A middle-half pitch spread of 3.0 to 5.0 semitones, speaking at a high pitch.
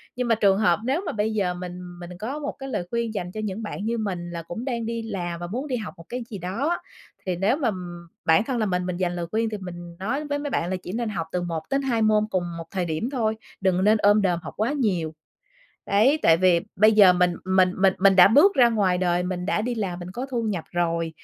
Yes: average, 4.5 semitones; high, 200 Hz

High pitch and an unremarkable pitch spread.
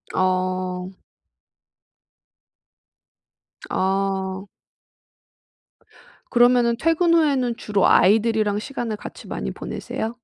Yes: high, 215 Hz; average, 4.3 semitones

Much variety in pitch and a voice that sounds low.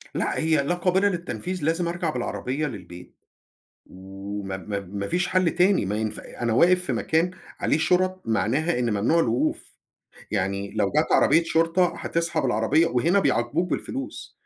No: wide, 8.6 semitones; medium, 155 Hz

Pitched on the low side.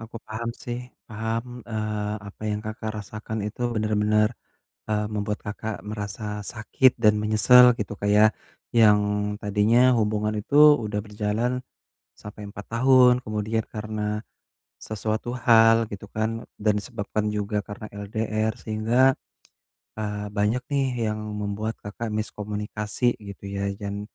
Yes: low, 105 Hz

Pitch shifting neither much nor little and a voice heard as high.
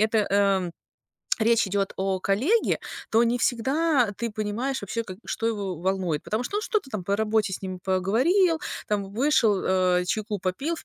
Yes: average, 4.3 semitones; high, 215 Hz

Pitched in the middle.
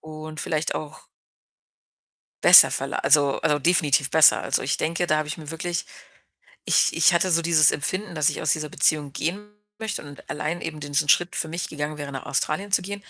Yes: medium, 155 Hz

